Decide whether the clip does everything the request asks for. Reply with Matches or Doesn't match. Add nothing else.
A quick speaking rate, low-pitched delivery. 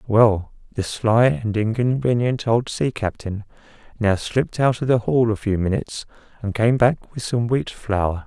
Doesn't match